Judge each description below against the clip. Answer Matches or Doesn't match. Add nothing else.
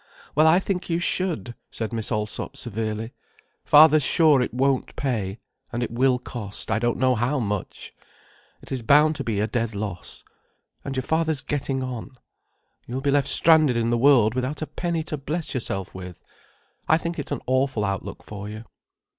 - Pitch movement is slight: Doesn't match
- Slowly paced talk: Doesn't match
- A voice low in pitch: Matches